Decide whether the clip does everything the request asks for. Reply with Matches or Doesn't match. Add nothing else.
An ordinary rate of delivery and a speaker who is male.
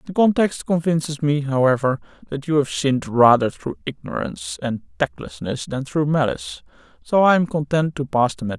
Matches